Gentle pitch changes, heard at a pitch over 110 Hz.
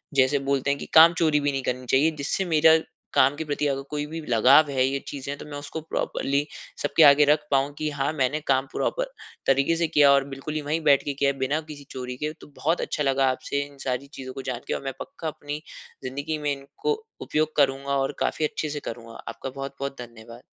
Yes: narrow, 2.0 semitones; medium, 140 Hz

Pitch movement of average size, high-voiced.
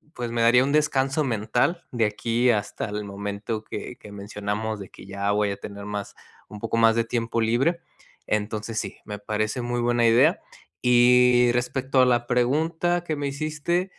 No: average, 3.7 semitones; low, 120 Hz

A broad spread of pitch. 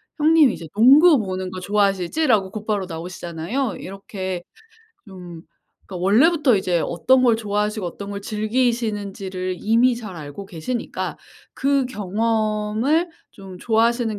No: average, 4.3 semitones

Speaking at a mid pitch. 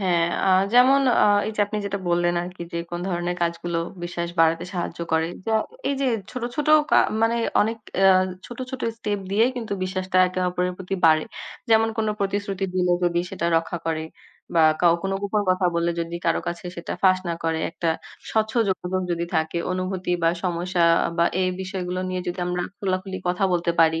Yes: medium, 180 Hz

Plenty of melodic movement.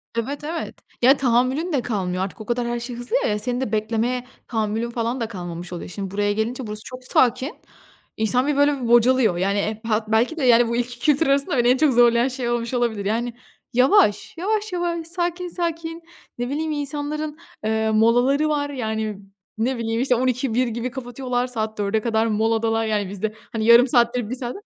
No: average, 3.5 semitones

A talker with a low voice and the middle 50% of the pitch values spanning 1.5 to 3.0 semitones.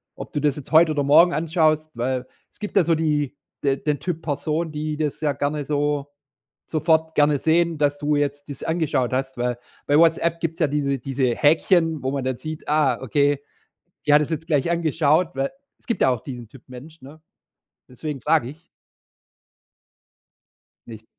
No: medium, 150 Hz; narrow, 2.6 semitones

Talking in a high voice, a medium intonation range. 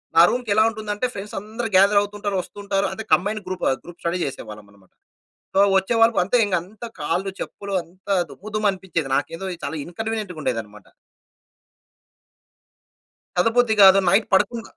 Yes: high, 195 Hz; average, 3.5 semitones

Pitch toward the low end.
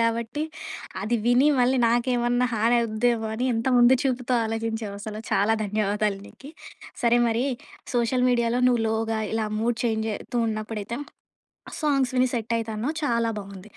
No: high, 230 Hz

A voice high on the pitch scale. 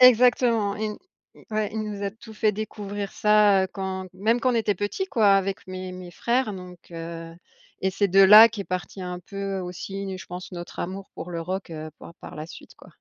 Yes: high, 195 Hz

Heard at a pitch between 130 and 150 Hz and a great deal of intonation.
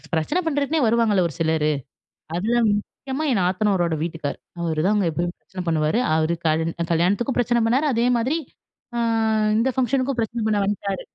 No: high, 205 Hz; wide, 6.3 semitones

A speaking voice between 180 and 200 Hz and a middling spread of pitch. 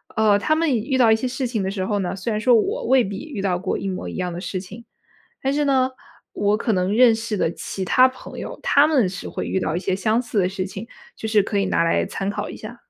No: high, 215 Hz; average, 4.9 semitones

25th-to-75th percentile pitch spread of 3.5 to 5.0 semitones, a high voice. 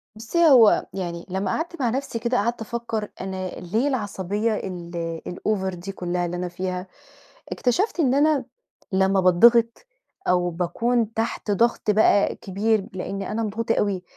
Yes: average, 4.2 semitones; high, 205 Hz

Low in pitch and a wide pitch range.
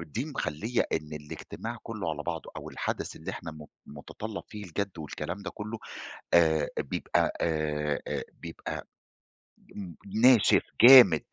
Yes: very low, 85 Hz; wide, 5.7 semitones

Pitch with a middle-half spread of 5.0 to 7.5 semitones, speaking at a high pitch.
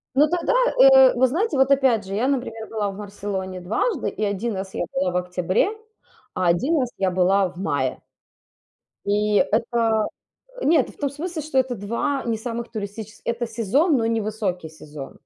Yes: wide, 5.6 semitones; high, 220 Hz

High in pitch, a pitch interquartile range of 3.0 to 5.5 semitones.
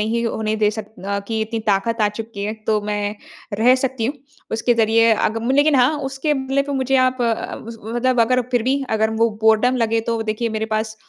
No: high, 230 Hz; narrow, 2.5 semitones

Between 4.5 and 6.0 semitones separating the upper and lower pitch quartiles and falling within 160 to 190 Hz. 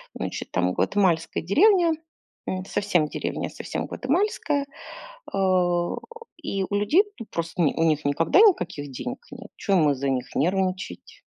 Yes: average, 4.9 semitones; medium, 185 Hz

